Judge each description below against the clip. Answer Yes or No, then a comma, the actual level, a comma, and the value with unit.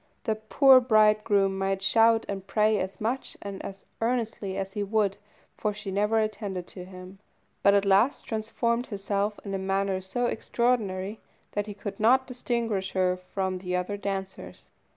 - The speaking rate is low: No, average, 165 wpm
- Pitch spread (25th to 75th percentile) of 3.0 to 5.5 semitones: No, narrow, 2.4 semitones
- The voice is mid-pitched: No, high, 205 Hz